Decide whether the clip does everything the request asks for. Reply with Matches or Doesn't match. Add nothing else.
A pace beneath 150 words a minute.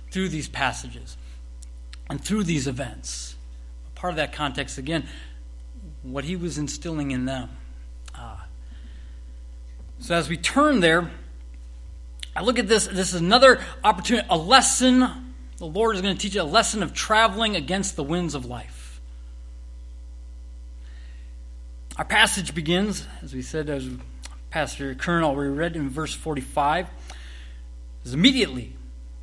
Matches